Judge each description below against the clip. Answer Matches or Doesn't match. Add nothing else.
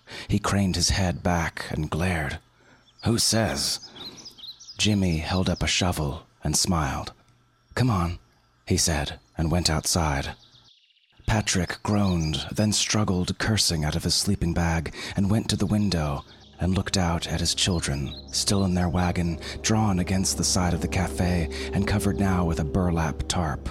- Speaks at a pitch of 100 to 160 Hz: Doesn't match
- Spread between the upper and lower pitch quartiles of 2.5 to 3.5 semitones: Doesn't match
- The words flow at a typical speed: Matches